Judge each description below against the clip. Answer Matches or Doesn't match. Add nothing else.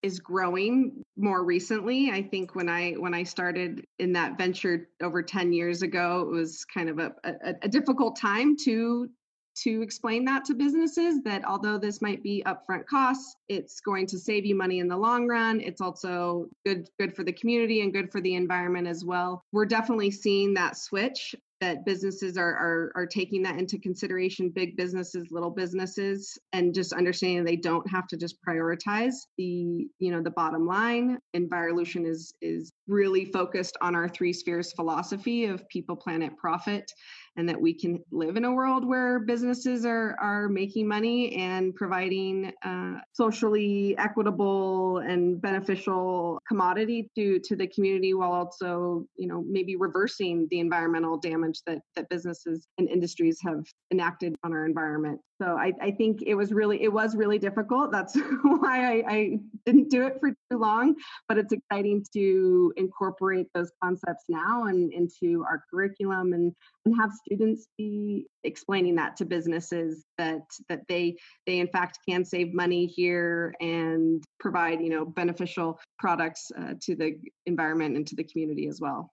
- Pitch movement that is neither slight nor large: Matches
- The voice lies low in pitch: Doesn't match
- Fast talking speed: Doesn't match